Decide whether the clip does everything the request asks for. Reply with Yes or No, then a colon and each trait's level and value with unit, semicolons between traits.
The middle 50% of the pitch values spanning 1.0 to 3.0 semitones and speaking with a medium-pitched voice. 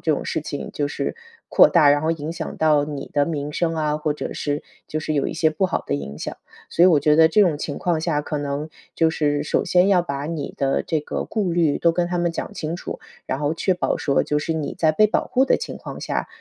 Yes: narrow, 2.4 semitones; medium, 155 Hz